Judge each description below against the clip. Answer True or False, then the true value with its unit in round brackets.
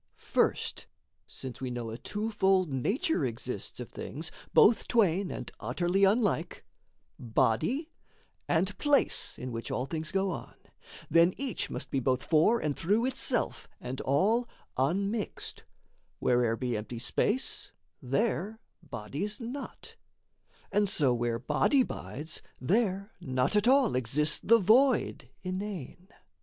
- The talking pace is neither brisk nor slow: False (125 wpm)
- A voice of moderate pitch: True (180 Hz)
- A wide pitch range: True (8.8 semitones)